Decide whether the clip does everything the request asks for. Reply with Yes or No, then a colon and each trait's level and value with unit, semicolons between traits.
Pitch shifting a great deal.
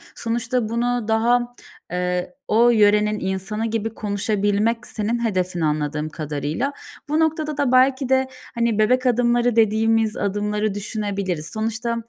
No: average, 3.0 semitones